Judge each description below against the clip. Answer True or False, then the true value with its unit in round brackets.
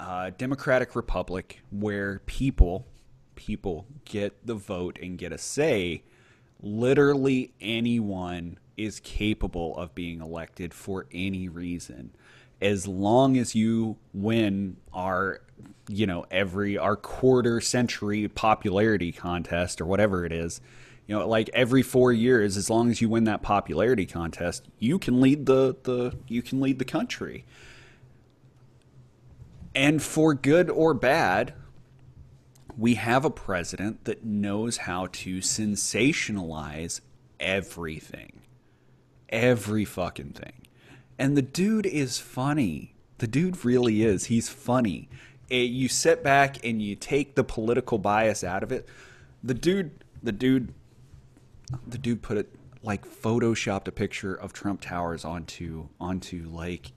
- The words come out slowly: True (130 wpm)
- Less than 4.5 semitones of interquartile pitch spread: False (5.3 semitones)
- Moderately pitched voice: False (110 Hz)